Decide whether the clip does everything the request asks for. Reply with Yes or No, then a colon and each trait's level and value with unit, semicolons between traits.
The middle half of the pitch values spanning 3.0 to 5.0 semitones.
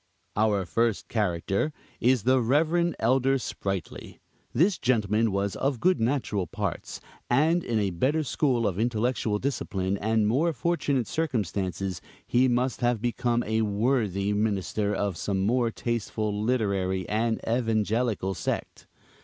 Yes: average, 4.0 semitones